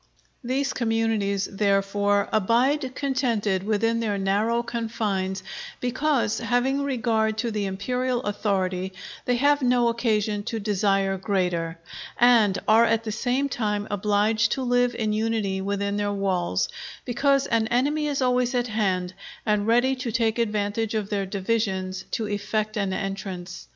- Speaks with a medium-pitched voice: No, high, 215 Hz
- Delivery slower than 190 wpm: Yes, average, 140 wpm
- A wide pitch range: No, average, 3.3 semitones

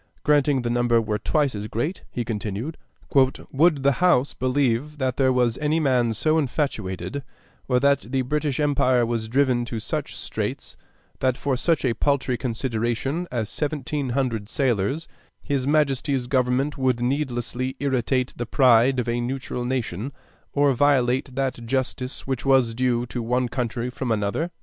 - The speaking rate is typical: Yes, average, 155 wpm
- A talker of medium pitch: No, low, 130 Hz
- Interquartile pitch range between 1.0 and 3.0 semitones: Yes, average, 2.7 semitones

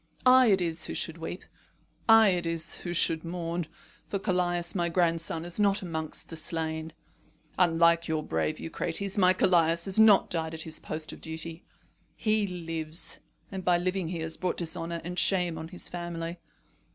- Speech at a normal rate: Yes, average, 175 wpm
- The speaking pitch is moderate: Yes, medium, 170 Hz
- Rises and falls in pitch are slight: Yes, narrow, 1.9 semitones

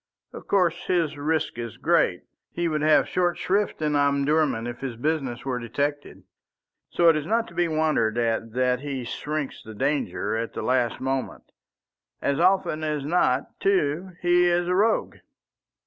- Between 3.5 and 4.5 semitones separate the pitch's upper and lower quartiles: No, average, 5.1 semitones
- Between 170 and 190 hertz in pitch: No, medium, 150 Hz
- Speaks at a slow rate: No, average, 165 wpm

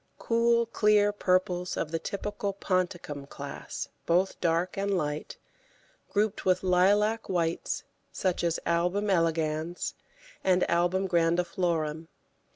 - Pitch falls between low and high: Yes, medium, 180 Hz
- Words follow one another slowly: Yes, slow, 110 wpm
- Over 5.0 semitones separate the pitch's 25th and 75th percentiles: No, average, 3.1 semitones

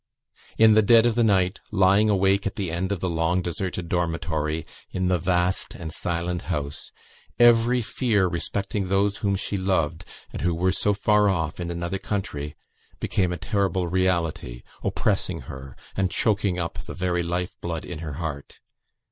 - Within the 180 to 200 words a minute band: No, average, 170 wpm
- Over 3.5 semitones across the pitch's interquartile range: No, average, 2.8 semitones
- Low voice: Yes, very low, 90 Hz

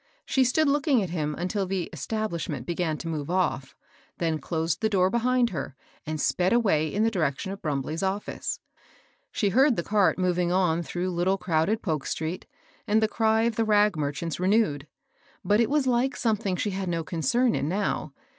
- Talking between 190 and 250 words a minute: Yes, average, 195 wpm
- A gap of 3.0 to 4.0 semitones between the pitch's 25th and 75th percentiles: No, average, 5.1 semitones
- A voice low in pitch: No, medium, 185 Hz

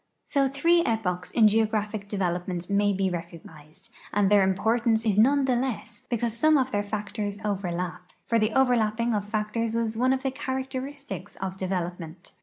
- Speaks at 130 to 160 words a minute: No, average, 175 wpm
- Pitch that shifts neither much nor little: Yes, average, 3.9 semitones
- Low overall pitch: No, high, 215 Hz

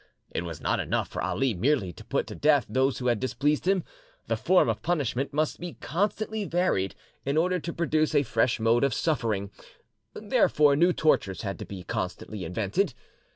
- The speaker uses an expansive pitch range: Yes, wide, 6.9 semitones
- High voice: No, medium, 140 Hz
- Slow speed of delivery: No, average, 180 wpm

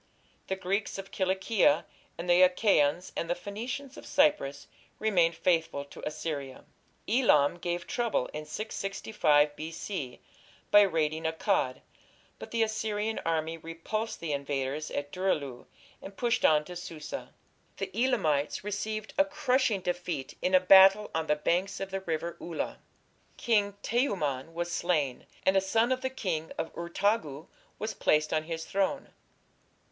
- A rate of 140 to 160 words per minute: Yes, average, 145 wpm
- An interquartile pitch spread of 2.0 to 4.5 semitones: No, average, 5.2 semitones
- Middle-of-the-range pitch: Yes, medium, 180 Hz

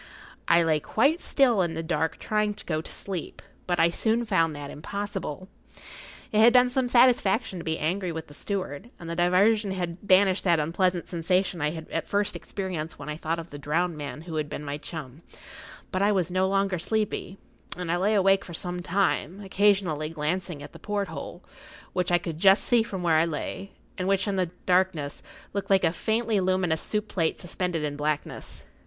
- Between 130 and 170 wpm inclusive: No, average, 200 wpm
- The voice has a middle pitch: Yes, medium, 180 Hz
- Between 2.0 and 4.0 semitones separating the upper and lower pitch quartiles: Yes, average, 3.6 semitones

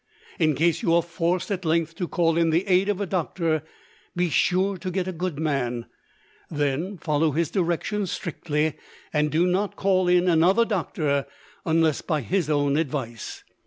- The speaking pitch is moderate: Yes, medium, 165 Hz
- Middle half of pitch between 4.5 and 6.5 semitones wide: No, average, 3.1 semitones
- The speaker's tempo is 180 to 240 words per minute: No, average, 170 wpm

